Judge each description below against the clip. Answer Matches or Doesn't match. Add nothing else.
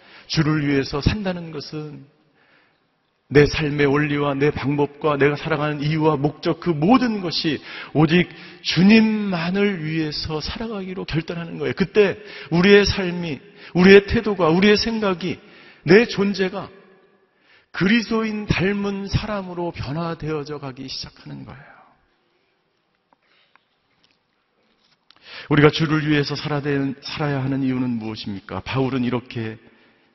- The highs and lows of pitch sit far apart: Doesn't match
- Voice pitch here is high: Doesn't match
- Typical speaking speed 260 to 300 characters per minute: Matches